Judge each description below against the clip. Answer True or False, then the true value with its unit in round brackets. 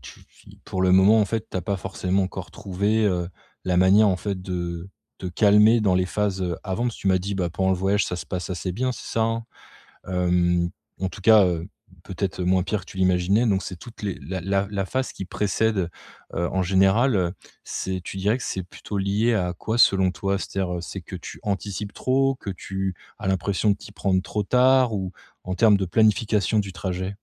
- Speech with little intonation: True (2.3 semitones)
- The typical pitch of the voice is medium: False (95 Hz)